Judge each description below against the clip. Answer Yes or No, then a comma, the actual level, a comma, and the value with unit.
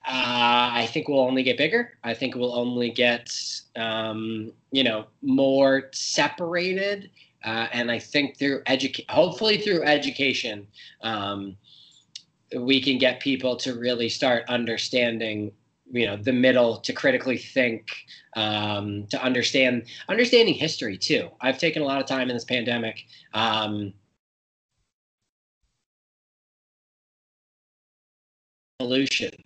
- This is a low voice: Yes, low, 125 Hz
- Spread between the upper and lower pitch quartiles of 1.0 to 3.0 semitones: No, average, 3.4 semitones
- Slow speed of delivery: Yes, slow, 120 wpm